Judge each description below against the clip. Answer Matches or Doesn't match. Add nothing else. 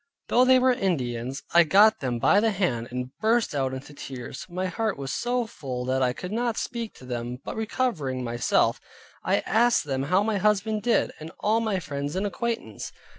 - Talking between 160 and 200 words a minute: Matches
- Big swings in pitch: Matches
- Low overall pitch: Doesn't match